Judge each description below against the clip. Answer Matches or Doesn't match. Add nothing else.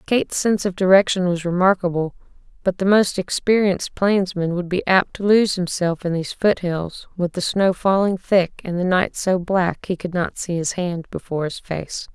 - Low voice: Doesn't match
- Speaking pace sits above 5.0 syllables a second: Doesn't match